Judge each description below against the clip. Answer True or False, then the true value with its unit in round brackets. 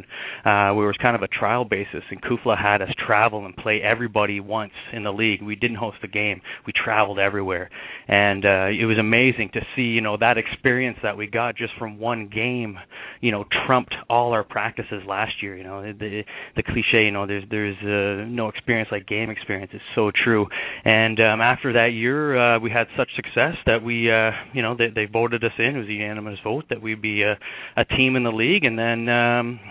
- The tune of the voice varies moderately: False (2.3 semitones)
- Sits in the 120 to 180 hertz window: False (110 Hz)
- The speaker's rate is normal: False (220 wpm)